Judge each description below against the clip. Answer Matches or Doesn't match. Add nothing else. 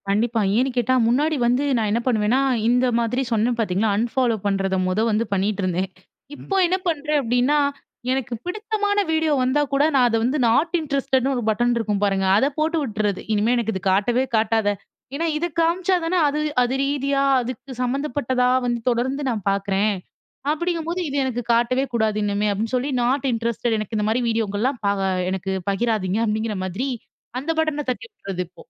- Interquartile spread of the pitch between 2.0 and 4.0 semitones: Doesn't match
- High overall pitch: Matches